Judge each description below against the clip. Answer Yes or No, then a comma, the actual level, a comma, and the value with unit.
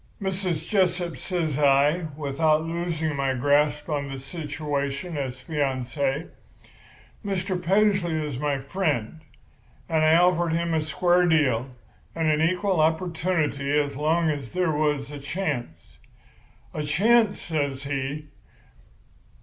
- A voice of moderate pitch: Yes, medium, 155 Hz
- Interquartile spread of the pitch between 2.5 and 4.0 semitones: Yes, average, 3.6 semitones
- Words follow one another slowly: Yes, slow, 125 wpm